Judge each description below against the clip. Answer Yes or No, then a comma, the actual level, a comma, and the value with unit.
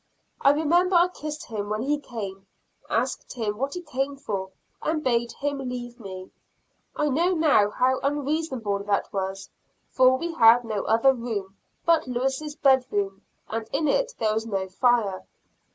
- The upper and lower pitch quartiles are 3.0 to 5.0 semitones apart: No, wide, 5.6 semitones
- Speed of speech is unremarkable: Yes, average, 165 wpm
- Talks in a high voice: Yes, very high, 250 Hz